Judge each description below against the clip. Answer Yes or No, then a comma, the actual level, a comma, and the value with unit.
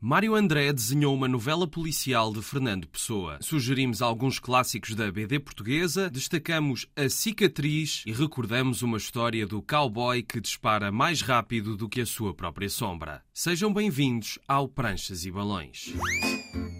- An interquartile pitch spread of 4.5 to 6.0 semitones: Yes, average, 5.2 semitones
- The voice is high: No, low, 125 Hz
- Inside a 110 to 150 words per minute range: Yes, average, 145 wpm